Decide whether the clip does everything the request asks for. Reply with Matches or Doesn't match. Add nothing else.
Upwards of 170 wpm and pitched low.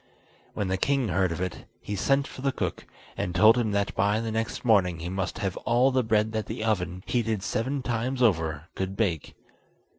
Matches